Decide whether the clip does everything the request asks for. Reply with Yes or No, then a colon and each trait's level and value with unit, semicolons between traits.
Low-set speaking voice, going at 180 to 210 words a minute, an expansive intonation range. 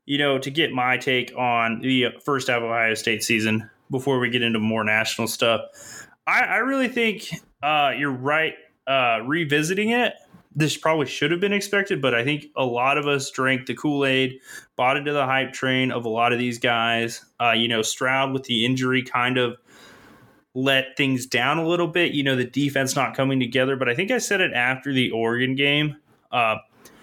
No: low, 130 Hz; fast, 205 wpm; average, 3.3 semitones